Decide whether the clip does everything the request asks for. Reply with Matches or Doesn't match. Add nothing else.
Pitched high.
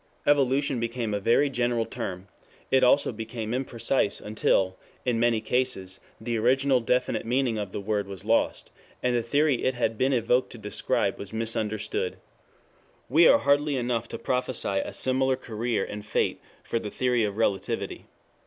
Doesn't match